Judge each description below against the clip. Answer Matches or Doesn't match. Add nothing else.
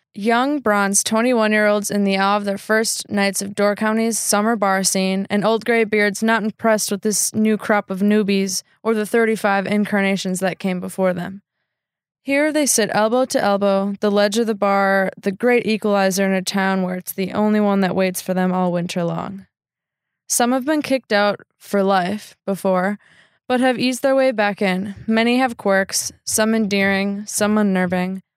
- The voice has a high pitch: Matches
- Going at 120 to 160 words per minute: Doesn't match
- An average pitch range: Doesn't match